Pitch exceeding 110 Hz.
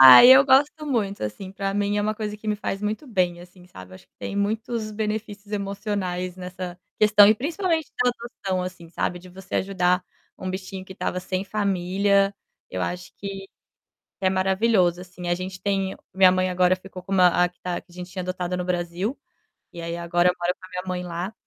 Yes: high, 190 Hz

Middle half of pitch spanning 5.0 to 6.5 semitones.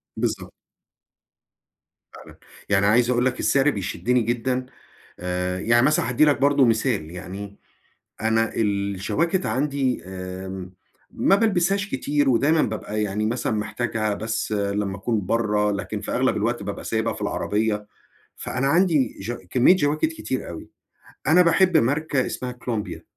Yes: wide, 5.5 semitones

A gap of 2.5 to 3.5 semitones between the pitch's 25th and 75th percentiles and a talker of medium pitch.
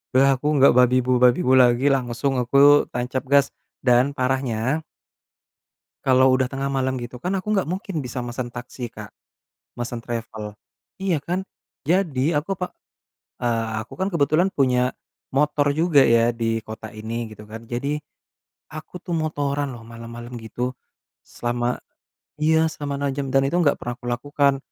No: average, 3.2 semitones; low, 130 Hz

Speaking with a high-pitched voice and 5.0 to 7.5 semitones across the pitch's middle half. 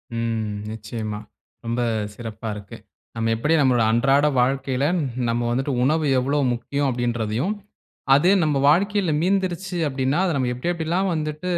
No: low, 135 Hz; wide, 5.4 semitones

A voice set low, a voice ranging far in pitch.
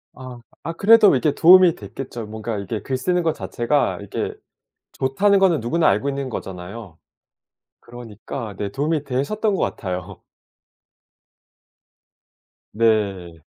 Yes: low, 125 Hz; wide, 7.4 semitones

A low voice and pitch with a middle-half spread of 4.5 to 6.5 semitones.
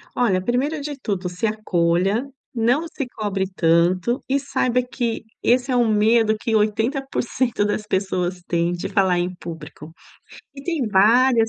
No: high, 220 Hz; average, 5.2 semitones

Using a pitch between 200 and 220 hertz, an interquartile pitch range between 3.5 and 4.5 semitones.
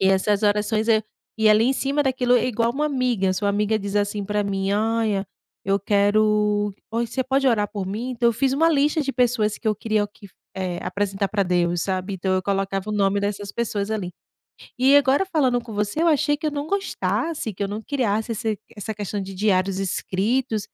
Yes: high, 210 Hz; average, 3.8 semitones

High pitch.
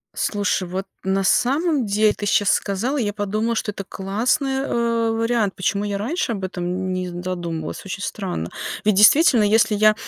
Yes: high, 205 Hz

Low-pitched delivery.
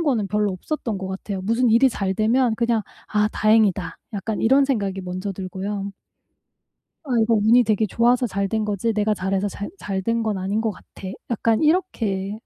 No: high, 210 Hz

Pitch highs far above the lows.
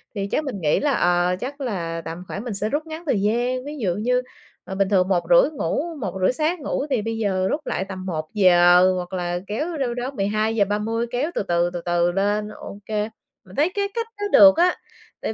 Yes: wide, 6.6 semitones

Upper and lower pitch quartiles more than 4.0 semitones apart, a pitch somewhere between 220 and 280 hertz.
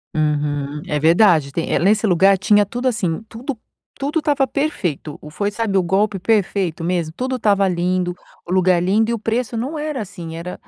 No: average, 4.9 semitones; high, 195 Hz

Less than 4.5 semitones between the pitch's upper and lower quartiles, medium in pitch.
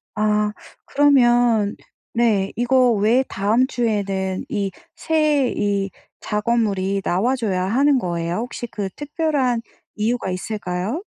No: average, 4.1 semitones; high, 220 Hz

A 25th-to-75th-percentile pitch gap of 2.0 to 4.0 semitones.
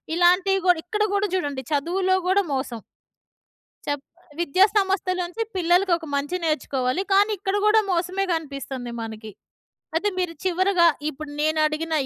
No: average, 4.6 semitones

